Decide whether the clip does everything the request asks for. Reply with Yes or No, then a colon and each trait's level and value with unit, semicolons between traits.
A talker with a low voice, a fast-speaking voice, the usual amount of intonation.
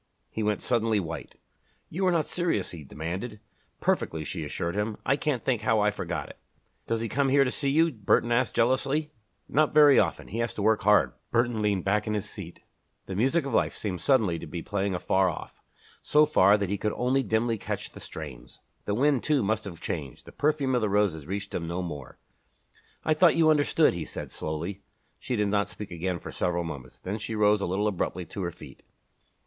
No: low, 105 Hz; fast, 215 wpm; wide, 5.9 semitones